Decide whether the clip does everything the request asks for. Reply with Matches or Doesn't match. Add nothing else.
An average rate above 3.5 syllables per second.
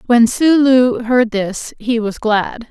Doesn't match